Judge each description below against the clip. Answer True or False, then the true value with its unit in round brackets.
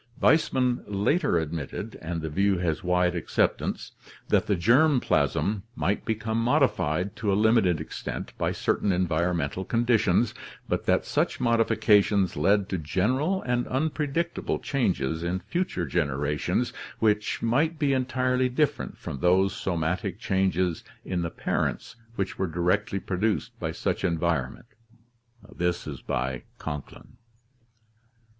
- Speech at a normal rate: False (120 wpm)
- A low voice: True (95 Hz)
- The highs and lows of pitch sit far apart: True (5.7 semitones)